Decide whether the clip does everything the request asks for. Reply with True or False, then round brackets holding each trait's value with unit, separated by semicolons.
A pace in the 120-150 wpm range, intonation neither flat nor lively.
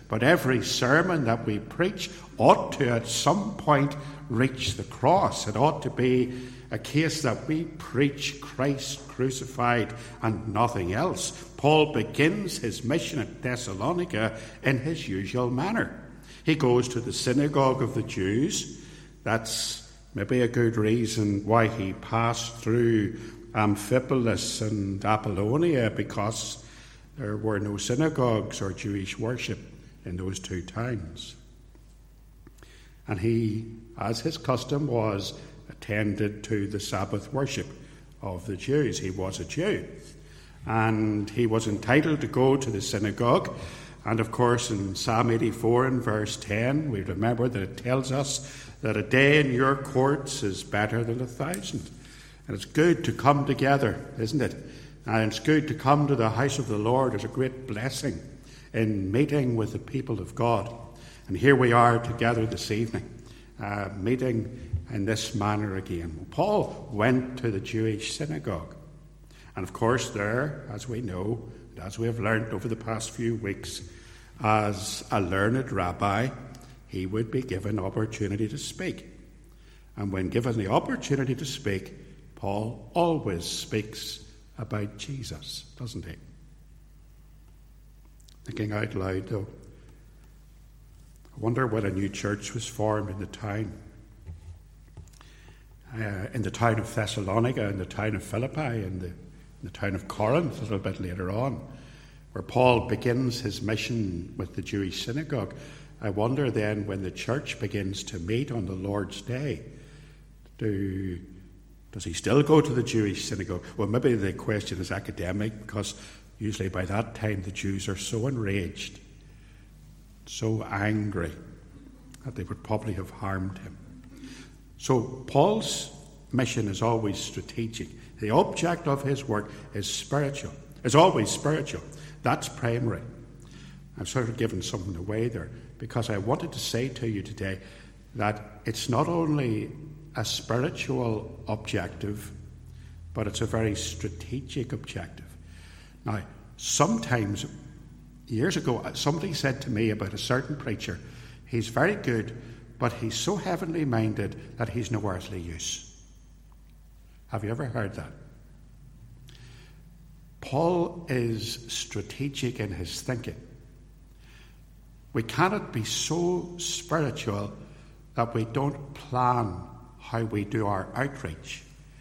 True (140 wpm; 4.2 semitones)